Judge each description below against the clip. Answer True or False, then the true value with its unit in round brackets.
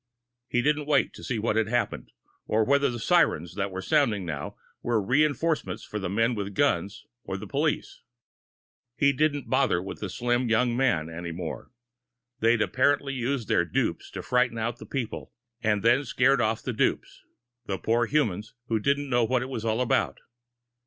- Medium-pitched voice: False (120 Hz)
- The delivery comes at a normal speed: True (185 wpm)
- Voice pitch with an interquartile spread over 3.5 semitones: True (4.2 semitones)